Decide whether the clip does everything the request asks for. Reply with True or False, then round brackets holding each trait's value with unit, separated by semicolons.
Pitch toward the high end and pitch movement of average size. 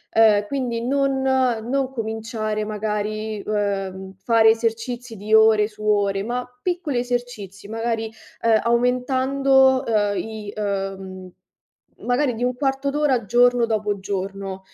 True (225 Hz; 3.2 semitones)